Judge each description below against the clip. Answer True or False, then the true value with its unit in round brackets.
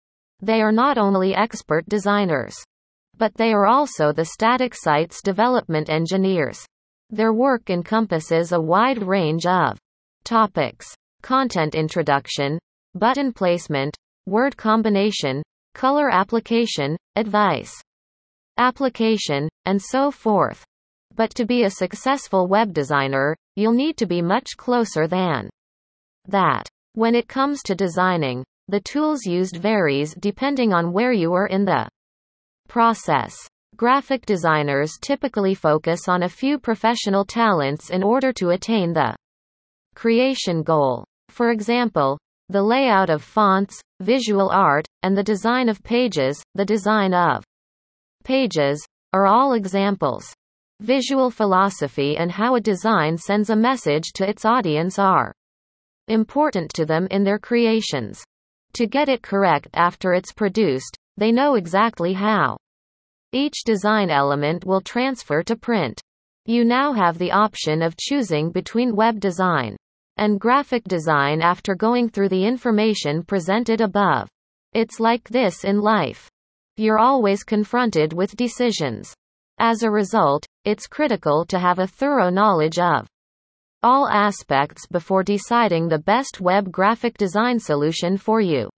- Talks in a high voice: True (200 Hz)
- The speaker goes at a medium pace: False (130 wpm)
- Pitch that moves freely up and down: True (5.7 semitones)